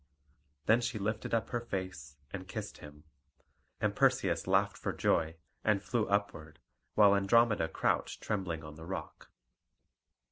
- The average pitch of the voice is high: No, low, 100 Hz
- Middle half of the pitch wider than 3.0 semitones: Yes, average, 5.1 semitones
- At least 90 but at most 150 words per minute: Yes, average, 140 wpm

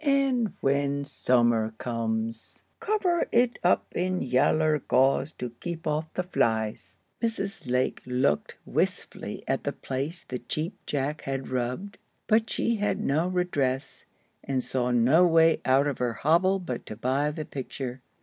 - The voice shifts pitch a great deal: Yes, wide, 6.1 semitones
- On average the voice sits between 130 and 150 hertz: Yes, medium, 140 Hz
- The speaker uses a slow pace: No, average, 150 wpm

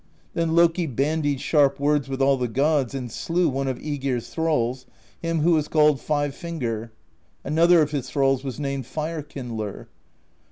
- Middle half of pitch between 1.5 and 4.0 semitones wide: Yes, average, 3.1 semitones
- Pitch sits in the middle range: Yes, medium, 145 Hz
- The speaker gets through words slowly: No, average, 165 wpm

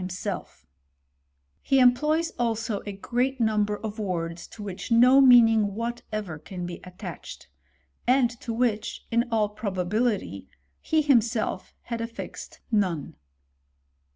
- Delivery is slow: Yes, slow, 125 wpm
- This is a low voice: No, high, 220 Hz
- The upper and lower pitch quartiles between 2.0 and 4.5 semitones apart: Yes, average, 3.4 semitones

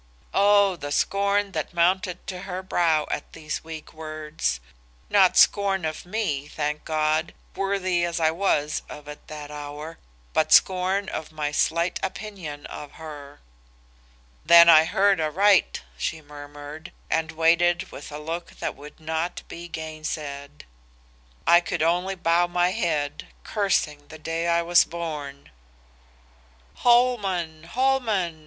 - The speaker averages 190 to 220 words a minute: No, slow, 135 wpm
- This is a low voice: No, medium, 165 Hz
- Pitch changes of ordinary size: Yes, average, 3.3 semitones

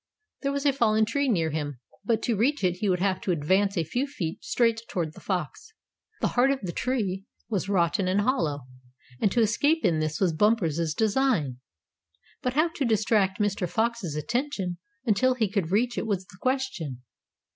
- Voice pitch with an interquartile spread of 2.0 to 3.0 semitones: No, wide, 5.6 semitones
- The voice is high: Yes, high, 205 Hz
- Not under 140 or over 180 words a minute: No, average, 190 wpm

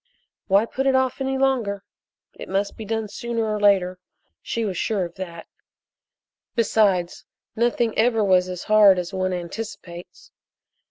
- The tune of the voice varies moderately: Yes, average, 3.6 semitones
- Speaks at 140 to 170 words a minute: Yes, average, 150 wpm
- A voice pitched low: No, high, 205 Hz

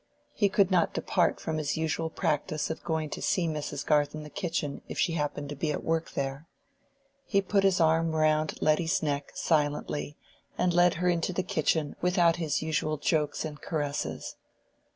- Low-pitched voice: No, medium, 160 Hz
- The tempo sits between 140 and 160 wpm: No, average, 180 wpm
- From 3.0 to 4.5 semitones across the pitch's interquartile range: No, narrow, 2.4 semitones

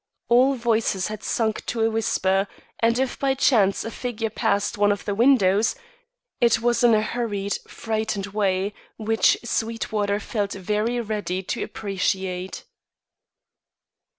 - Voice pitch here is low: No, high, 215 Hz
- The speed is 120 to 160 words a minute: Yes, slow, 135 wpm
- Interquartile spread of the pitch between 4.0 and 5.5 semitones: No, narrow, 2.6 semitones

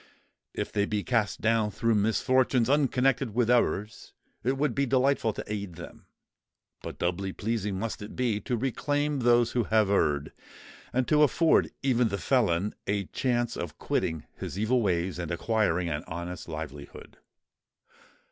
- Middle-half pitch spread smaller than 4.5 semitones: No, average, 4.9 semitones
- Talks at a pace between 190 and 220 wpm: No, average, 155 wpm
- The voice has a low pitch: Yes, low, 110 Hz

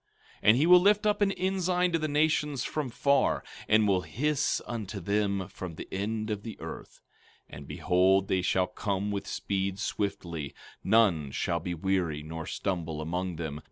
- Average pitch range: No, wide, 7.5 semitones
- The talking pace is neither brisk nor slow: Yes, average, 175 wpm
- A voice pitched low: Yes, low, 100 Hz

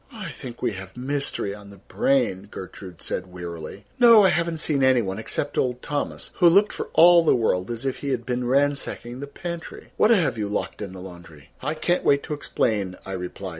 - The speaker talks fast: Yes, fast, 210 wpm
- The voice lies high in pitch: No, low, 125 Hz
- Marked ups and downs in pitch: Yes, wide, 8.2 semitones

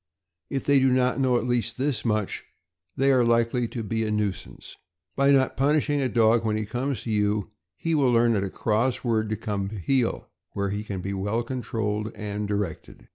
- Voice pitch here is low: Yes, low, 115 Hz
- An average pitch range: Yes, average, 3.5 semitones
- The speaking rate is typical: No, fast, 210 wpm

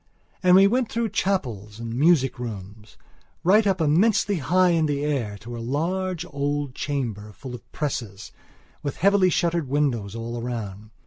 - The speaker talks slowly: No, average, 155 wpm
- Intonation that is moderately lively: No, wide, 7.6 semitones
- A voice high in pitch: No, medium, 145 Hz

